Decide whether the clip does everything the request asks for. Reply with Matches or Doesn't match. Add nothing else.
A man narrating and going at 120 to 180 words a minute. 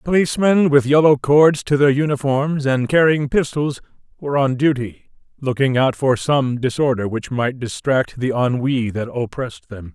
Matches